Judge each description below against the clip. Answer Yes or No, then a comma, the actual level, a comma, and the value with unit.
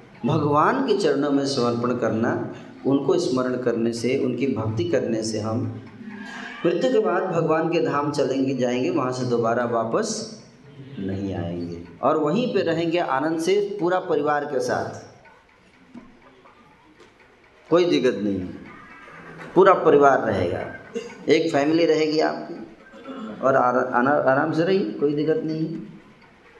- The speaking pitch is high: No, medium, 140 Hz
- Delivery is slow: No, average, 135 wpm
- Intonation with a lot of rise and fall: Yes, wide, 5.8 semitones